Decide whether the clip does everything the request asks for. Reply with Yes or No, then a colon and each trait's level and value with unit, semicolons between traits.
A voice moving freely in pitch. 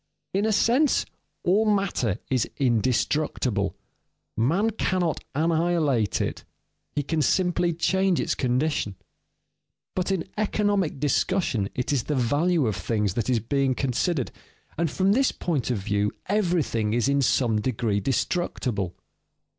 Yes: wide, 7.3 semitones